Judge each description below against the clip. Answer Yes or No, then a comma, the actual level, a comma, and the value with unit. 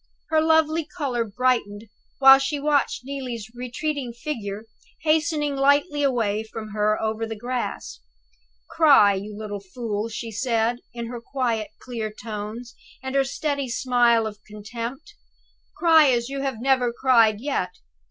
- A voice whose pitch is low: No, high, 240 Hz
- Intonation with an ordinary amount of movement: Yes, average, 4.2 semitones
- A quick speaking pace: No, average, 140 wpm